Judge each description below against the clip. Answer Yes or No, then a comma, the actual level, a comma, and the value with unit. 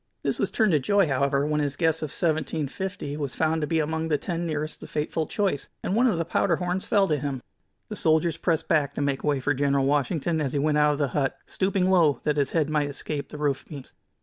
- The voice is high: No, medium, 150 Hz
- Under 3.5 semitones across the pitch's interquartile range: Yes, average, 2.7 semitones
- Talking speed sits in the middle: No, fast, 245 wpm